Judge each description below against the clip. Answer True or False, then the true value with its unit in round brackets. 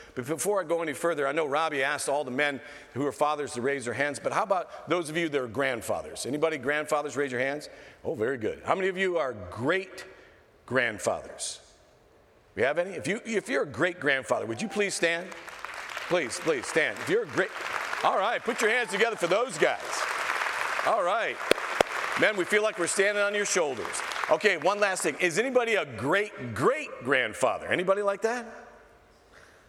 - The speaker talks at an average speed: True (195 wpm)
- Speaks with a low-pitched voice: False (170 Hz)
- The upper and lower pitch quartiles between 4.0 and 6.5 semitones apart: True (5.4 semitones)